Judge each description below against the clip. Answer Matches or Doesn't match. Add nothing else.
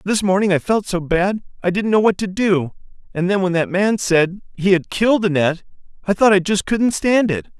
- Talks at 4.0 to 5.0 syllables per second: Doesn't match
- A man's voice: Matches